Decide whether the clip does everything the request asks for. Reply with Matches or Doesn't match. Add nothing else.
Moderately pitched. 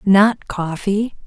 Doesn't match